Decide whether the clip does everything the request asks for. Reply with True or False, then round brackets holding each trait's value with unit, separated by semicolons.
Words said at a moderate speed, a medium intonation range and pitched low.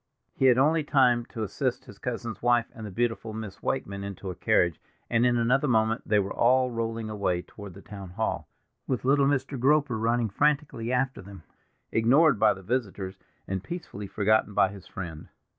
True (185 wpm; 4.4 semitones; 115 Hz)